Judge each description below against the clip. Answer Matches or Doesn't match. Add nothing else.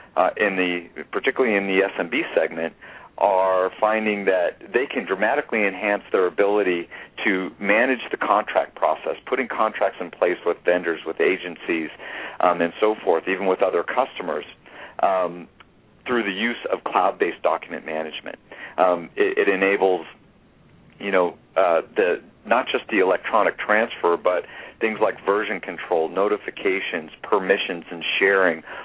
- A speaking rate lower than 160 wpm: Matches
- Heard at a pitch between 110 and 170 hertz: Doesn't match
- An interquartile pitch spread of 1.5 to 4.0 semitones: Matches